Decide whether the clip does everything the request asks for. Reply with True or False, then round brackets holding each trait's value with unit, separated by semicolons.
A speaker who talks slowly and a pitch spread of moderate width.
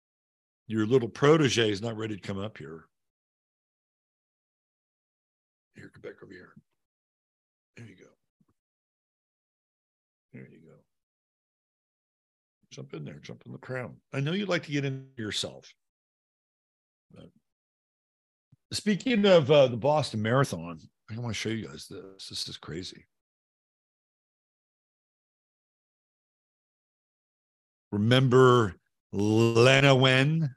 True (110 wpm; 5.0 semitones)